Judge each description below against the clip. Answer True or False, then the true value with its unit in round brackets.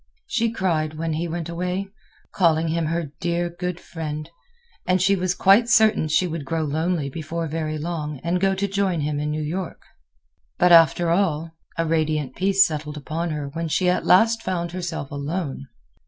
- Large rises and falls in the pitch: False (2.9 semitones)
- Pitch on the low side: False (165 Hz)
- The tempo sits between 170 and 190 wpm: True (180 wpm)